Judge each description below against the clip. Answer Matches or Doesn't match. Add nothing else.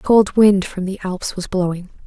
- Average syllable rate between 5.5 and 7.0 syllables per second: Doesn't match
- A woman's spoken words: Matches